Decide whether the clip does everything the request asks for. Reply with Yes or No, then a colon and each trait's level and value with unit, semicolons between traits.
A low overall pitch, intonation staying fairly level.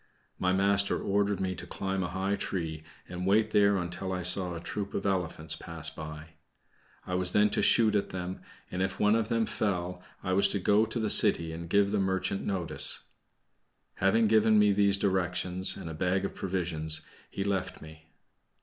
Yes: very low, 95 Hz; narrow, 2.3 semitones